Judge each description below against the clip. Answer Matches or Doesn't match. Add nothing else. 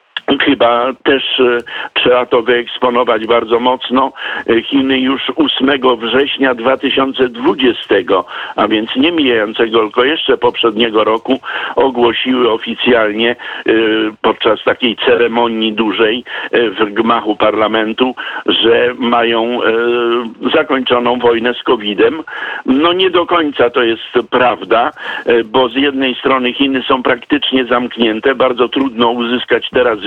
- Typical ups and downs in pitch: Doesn't match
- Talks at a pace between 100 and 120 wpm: Matches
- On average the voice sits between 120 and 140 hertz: Matches